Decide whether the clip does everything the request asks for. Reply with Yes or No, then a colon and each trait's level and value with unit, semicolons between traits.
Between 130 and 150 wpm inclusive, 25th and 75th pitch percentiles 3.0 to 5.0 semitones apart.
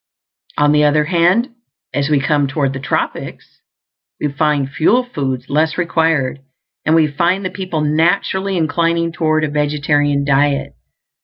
No: average, 145 wpm; narrow, 2.6 semitones